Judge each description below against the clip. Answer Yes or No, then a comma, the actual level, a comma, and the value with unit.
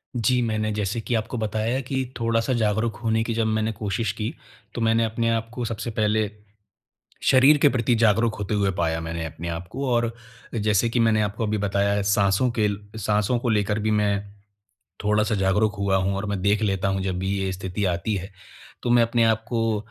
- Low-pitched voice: Yes, low, 110 Hz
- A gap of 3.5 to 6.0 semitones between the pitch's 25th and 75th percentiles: No, narrow, 2.5 semitones